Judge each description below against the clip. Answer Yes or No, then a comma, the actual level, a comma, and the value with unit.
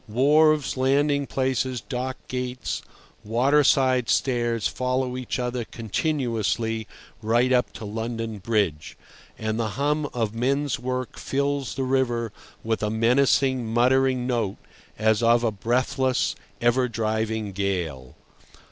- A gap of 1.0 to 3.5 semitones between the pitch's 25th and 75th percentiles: Yes, average, 2.9 semitones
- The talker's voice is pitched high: No, low, 125 Hz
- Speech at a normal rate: No, slow, 120 wpm